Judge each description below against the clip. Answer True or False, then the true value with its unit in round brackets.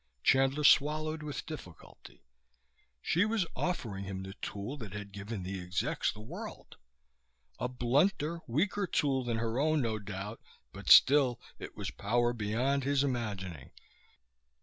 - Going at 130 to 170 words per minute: True (140 wpm)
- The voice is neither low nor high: False (120 Hz)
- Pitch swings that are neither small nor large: False (6.2 semitones)